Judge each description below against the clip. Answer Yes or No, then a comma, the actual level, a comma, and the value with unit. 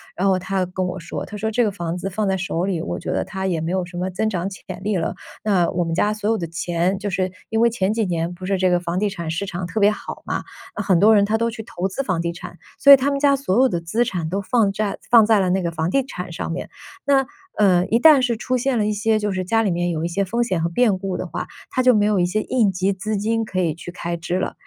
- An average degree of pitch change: Yes, average, 3.6 semitones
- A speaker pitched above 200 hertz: No, high, 190 Hz